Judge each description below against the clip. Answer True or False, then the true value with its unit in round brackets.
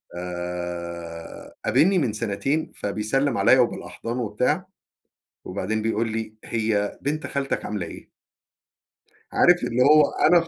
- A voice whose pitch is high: False (110 Hz)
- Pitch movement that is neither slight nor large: False (5.9 semitones)